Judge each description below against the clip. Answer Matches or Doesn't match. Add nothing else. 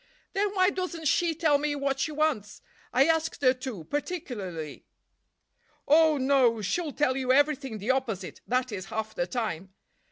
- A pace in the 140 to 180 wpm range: Matches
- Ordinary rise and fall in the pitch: Doesn't match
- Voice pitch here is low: Doesn't match